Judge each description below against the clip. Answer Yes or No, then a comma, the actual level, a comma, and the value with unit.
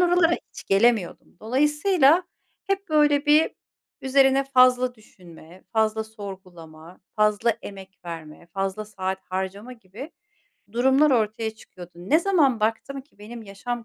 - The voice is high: Yes, high, 225 Hz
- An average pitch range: No, wide, 6.1 semitones